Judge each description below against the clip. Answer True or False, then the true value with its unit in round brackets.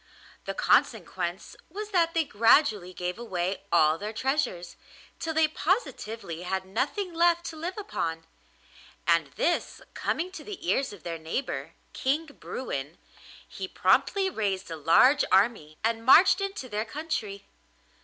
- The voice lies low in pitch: False (230 Hz)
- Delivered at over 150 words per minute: False (140 wpm)